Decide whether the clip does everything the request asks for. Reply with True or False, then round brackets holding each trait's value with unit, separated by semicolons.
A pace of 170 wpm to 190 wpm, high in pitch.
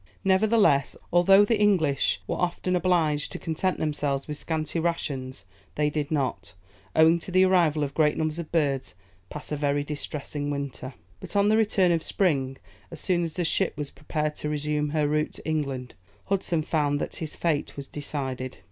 False (180 wpm; 150 Hz)